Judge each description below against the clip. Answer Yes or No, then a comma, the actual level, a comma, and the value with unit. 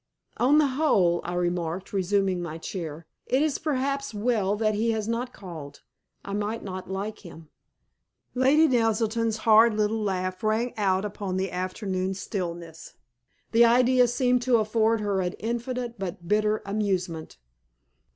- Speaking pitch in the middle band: No, high, 210 Hz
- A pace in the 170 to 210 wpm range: No, average, 140 wpm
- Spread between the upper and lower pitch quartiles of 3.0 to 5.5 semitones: Yes, average, 4.1 semitones